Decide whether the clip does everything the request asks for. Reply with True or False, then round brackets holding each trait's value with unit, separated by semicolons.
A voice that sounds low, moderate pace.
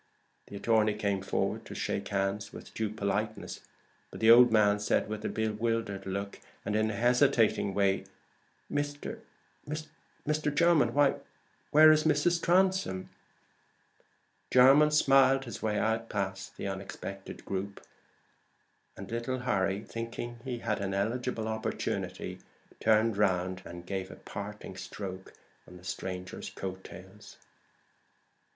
False (105 Hz; 130 wpm)